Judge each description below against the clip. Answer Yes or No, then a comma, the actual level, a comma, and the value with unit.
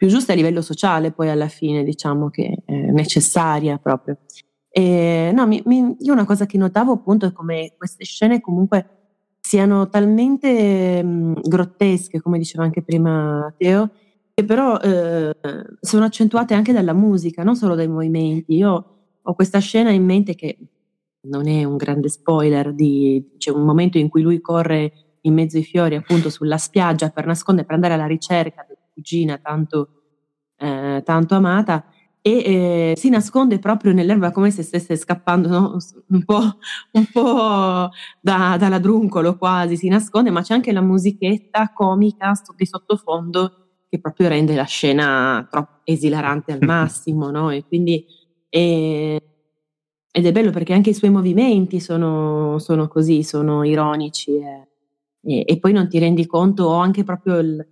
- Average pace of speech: Yes, average, 160 wpm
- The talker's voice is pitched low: No, medium, 170 Hz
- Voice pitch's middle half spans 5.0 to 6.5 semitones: No, average, 4.2 semitones